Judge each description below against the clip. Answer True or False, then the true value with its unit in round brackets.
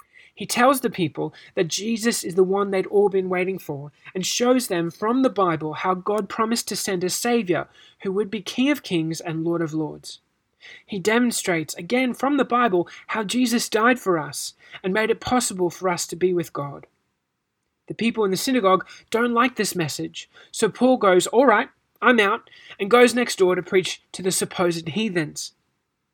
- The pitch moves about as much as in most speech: True (5.0 semitones)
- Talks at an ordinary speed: True (190 wpm)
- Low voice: False (195 Hz)